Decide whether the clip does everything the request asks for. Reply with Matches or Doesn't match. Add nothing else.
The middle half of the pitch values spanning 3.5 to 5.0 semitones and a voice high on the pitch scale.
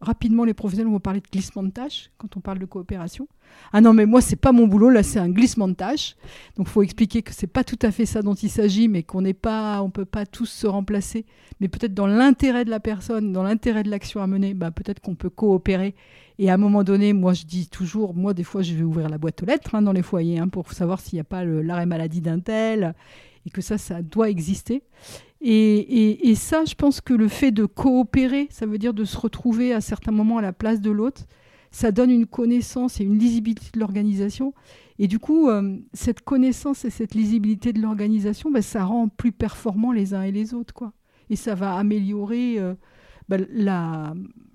Doesn't match